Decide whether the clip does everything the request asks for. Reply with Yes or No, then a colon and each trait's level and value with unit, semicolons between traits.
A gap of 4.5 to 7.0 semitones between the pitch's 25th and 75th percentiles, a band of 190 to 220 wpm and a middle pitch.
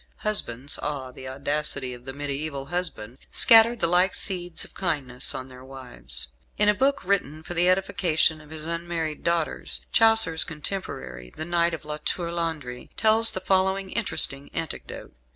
No: average, 5.2 semitones; average, 160 wpm; medium, 160 Hz